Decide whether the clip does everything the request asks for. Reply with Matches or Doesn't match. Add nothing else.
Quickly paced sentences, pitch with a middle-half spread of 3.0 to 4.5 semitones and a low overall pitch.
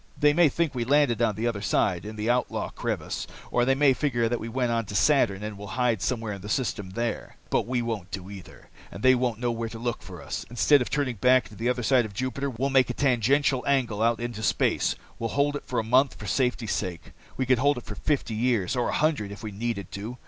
Matches